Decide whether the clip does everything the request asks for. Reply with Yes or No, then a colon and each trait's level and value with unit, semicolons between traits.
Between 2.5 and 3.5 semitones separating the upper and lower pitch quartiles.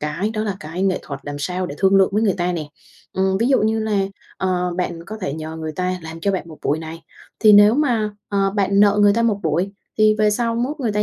No: average, 4.2 semitones